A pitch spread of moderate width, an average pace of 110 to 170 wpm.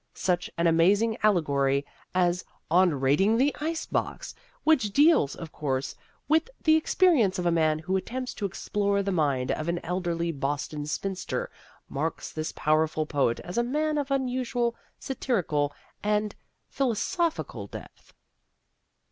No: wide, 8.1 semitones; average, 140 wpm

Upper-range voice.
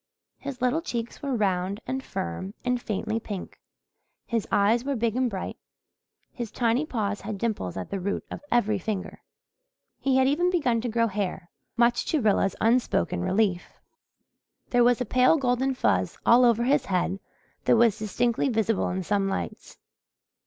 Yes: high, 230 Hz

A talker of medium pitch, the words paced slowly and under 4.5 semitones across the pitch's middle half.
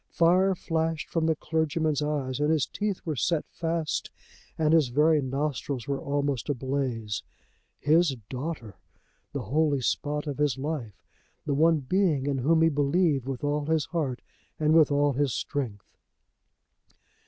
No: medium, 145 Hz; average, 150 wpm; average, 2.9 semitones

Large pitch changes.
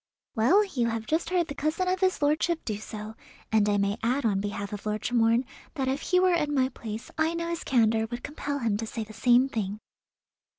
Yes: wide, 6.1 semitones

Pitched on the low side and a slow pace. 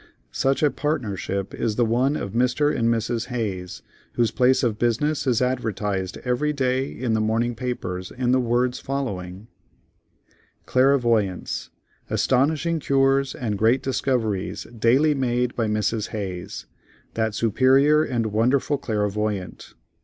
Yes: low, 120 Hz; slow, 125 wpm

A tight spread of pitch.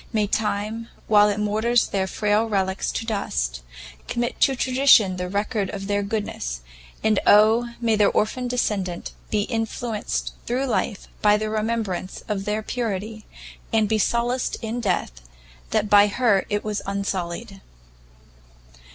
Yes: narrow, 2.2 semitones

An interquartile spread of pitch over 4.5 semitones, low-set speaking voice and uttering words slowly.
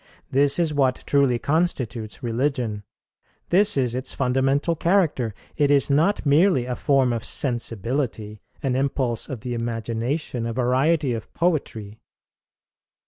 No: average, 3.6 semitones; low, 130 Hz; slow, 130 wpm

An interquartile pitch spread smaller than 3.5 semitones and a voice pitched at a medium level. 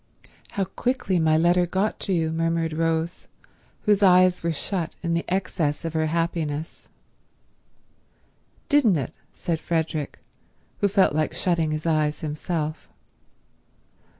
Yes: narrow, 2.6 semitones; medium, 165 Hz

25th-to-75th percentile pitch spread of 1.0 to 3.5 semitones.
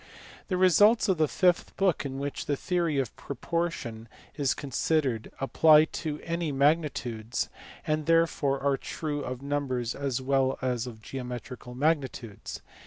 No: average, 4.0 semitones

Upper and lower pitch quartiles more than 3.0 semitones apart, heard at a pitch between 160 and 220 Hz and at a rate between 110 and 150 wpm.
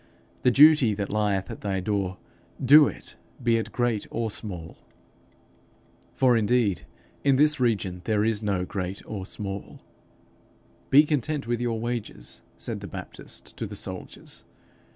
No: average, 3.9 semitones; low, 110 Hz; average, 145 wpm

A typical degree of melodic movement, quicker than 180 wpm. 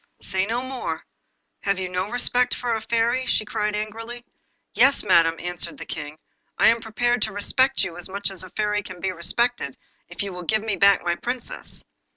Yes: average, 4.3 semitones; average, 195 wpm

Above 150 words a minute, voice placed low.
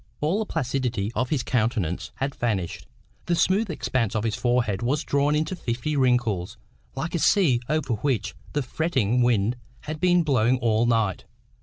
Yes: average, 165 wpm; low, 125 Hz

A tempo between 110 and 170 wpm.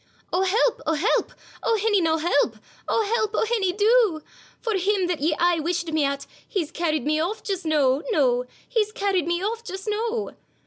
No: average, 190 wpm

